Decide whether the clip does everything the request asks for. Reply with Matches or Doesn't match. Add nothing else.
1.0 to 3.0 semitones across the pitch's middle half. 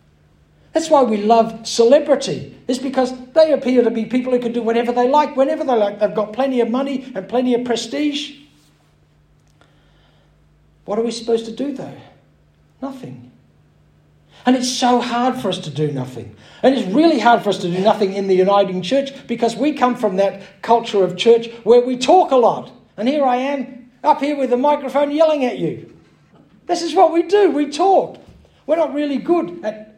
Doesn't match